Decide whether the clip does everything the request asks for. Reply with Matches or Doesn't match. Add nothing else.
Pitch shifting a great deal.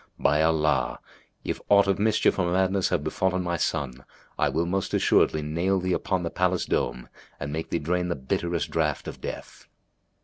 Doesn't match